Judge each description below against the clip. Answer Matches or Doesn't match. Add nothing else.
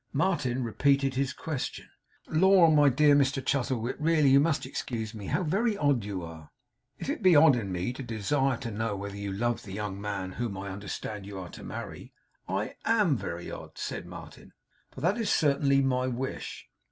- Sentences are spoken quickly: Doesn't match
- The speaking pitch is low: Matches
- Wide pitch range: Matches